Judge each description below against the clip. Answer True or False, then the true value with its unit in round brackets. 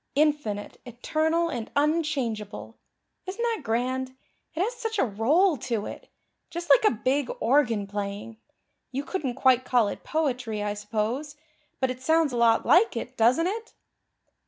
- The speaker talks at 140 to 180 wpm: True (155 wpm)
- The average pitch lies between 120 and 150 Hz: False (260 Hz)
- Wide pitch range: True (5.9 semitones)